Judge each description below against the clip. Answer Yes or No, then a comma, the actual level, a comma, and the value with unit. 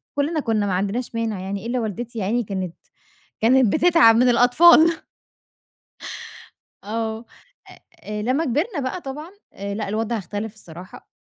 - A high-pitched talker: Yes, high, 230 Hz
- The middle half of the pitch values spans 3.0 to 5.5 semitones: Yes, average, 4.2 semitones